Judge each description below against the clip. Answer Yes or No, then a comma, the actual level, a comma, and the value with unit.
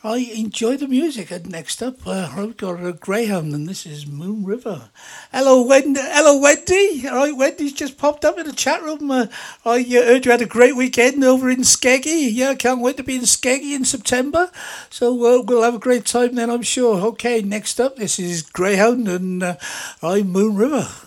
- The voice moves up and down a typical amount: Yes, average, 4.5 semitones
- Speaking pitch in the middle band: No, high, 245 Hz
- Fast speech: Yes, fast, 210 wpm